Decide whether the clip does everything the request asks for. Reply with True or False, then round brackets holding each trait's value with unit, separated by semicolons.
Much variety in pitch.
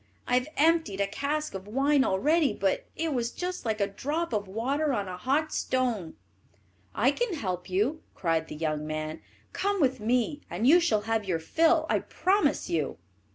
True (7.9 semitones)